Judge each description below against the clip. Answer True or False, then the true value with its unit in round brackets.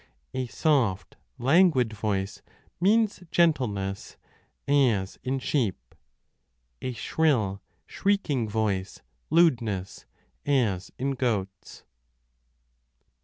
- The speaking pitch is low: True (120 Hz)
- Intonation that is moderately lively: False (6.5 semitones)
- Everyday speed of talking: False (80 wpm)